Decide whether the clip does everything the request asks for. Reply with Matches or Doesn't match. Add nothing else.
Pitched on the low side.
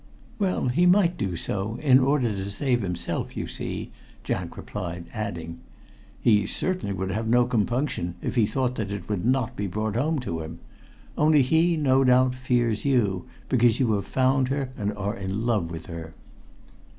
Matches